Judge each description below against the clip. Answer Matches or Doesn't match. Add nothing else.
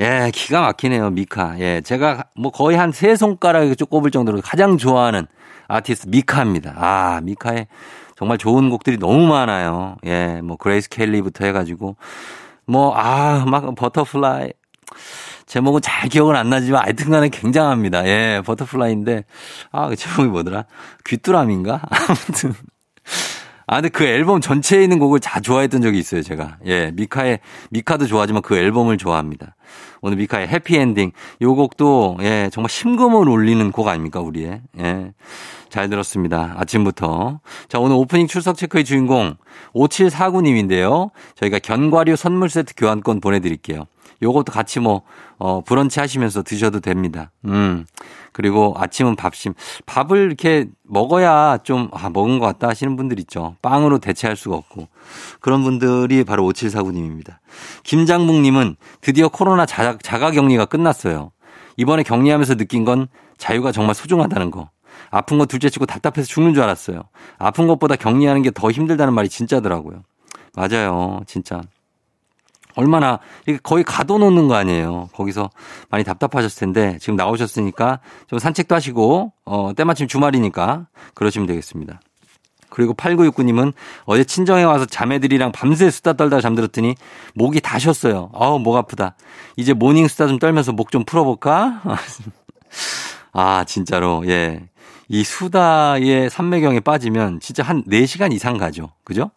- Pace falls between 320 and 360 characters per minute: Matches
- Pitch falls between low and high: Doesn't match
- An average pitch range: Doesn't match